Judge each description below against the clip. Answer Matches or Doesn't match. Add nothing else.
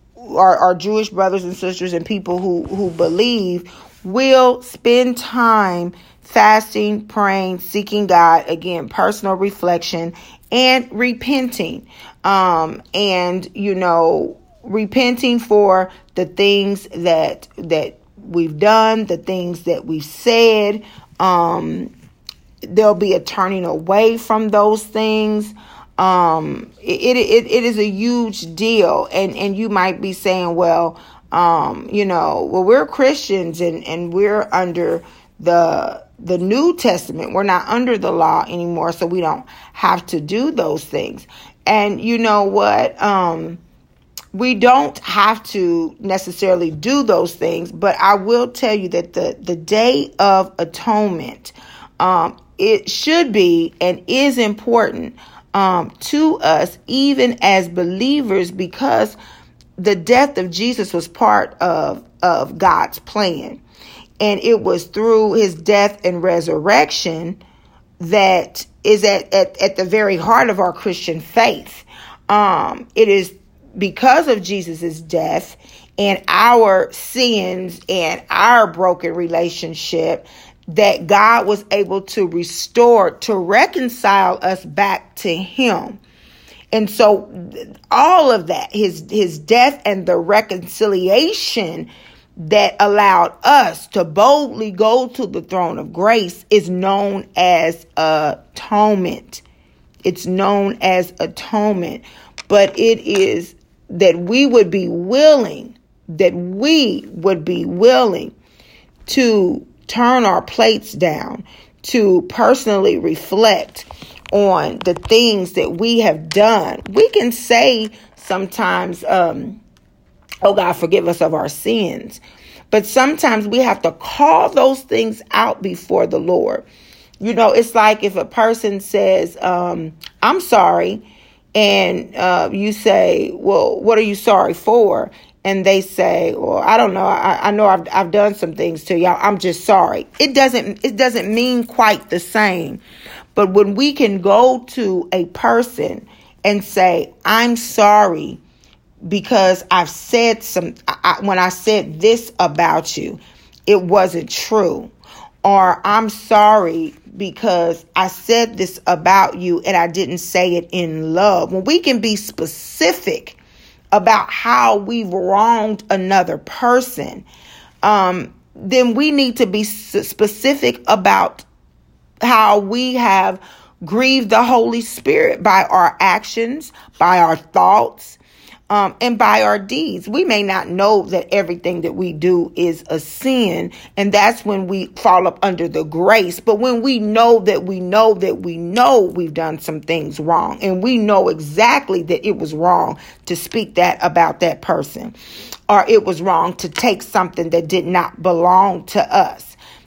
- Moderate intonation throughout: Matches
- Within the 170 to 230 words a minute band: Doesn't match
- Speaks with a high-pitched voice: Matches